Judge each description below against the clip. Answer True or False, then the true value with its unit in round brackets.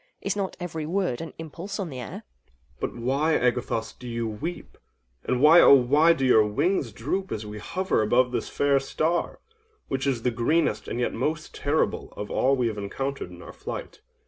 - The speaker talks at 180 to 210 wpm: True (190 wpm)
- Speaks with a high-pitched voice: False (135 Hz)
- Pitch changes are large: True (6.1 semitones)